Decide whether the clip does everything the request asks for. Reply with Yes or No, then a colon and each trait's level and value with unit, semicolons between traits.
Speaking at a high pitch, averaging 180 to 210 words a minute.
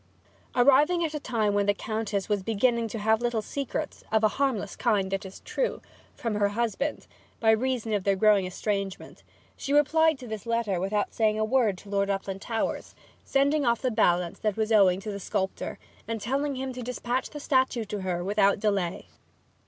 Yes: high, 220 Hz; average, 190 wpm